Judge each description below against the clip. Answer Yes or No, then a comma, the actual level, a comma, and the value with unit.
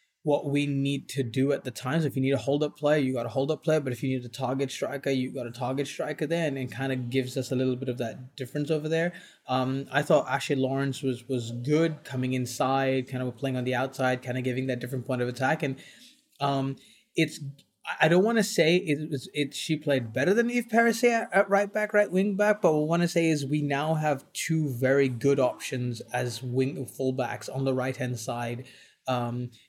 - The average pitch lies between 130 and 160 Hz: Yes, low, 135 Hz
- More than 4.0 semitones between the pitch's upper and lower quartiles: No, average, 3.2 semitones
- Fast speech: Yes, fast, 240 wpm